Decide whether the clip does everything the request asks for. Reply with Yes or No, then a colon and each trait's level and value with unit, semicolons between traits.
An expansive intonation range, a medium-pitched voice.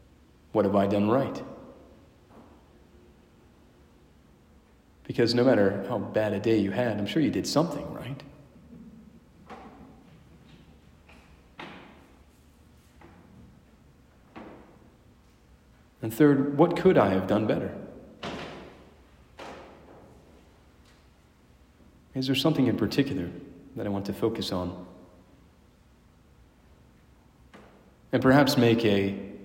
No: wide, 7.9 semitones; low, 100 Hz